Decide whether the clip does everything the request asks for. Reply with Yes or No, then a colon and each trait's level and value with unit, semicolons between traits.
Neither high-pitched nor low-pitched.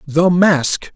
Yes: medium, 165 Hz